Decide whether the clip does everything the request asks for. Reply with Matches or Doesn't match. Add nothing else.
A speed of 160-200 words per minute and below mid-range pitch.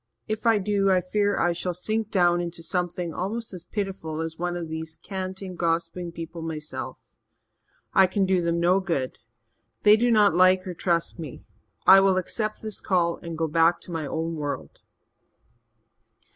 Doesn't match